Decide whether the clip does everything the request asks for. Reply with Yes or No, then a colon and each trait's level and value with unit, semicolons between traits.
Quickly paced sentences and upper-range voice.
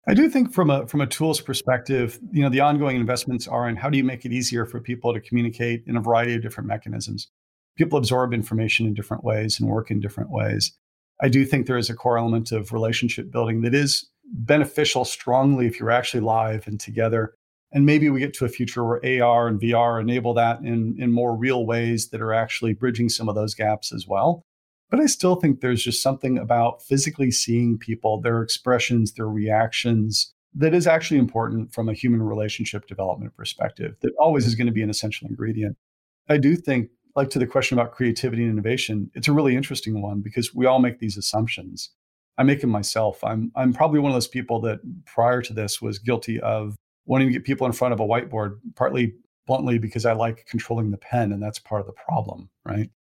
No: fast, 215 wpm; low, 120 Hz